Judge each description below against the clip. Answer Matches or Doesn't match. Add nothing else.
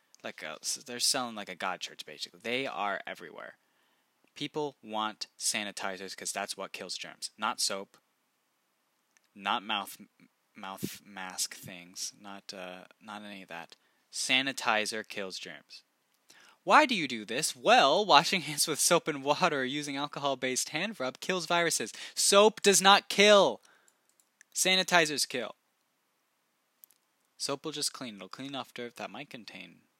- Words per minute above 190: Doesn't match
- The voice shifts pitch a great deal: Matches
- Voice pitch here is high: Doesn't match